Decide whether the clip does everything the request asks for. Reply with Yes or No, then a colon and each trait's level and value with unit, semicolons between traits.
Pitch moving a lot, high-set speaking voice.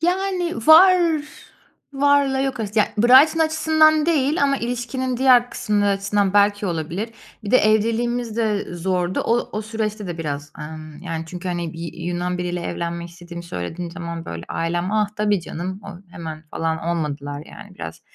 Yes: wide, 6.3 semitones; high, 200 Hz